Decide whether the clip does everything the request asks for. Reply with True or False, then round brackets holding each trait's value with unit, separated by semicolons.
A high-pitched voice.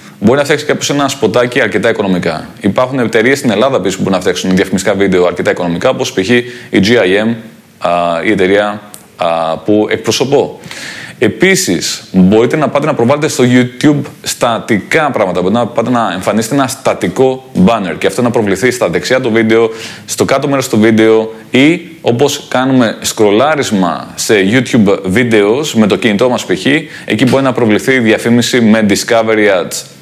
False (115 Hz)